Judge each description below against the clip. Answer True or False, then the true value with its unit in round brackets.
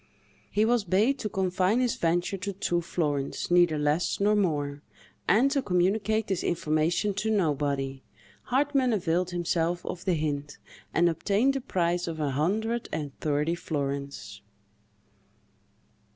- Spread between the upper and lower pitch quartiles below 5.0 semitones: False (5.3 semitones)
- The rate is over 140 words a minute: False (135 wpm)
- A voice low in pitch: False (175 Hz)